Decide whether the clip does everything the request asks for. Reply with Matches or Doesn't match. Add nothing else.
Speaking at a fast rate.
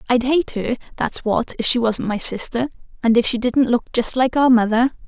Matches